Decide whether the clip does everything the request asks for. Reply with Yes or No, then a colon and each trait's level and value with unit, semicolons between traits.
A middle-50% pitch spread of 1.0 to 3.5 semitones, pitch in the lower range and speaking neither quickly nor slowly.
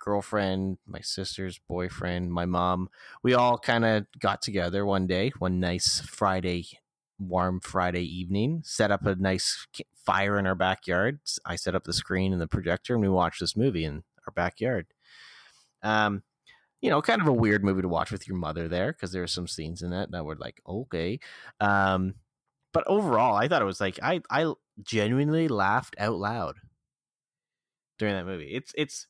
Yes: average, 3.1 semitones; very low, 95 Hz; average, 180 wpm